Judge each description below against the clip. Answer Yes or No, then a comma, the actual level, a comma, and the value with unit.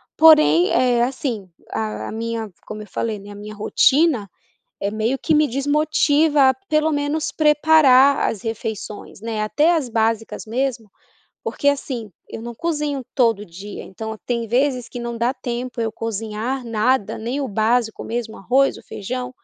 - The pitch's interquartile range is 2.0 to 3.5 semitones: No, average, 4.0 semitones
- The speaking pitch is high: Yes, high, 235 Hz